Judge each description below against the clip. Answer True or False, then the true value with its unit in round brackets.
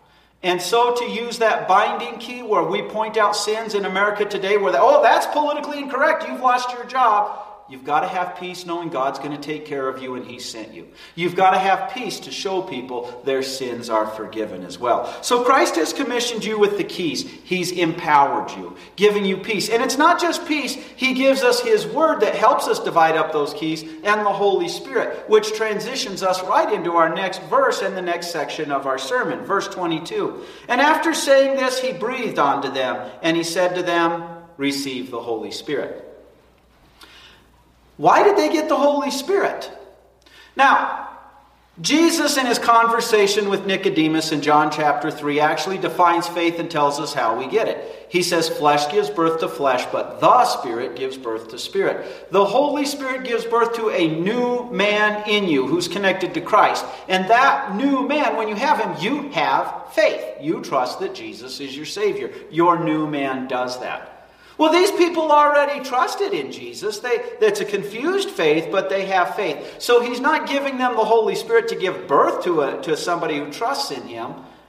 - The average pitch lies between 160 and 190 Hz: False (210 Hz)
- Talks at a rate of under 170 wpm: False (190 wpm)